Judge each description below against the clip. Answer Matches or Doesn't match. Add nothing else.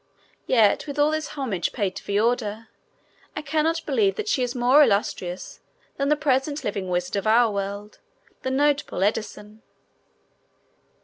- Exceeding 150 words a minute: Doesn't match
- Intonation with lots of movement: Matches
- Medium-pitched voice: Doesn't match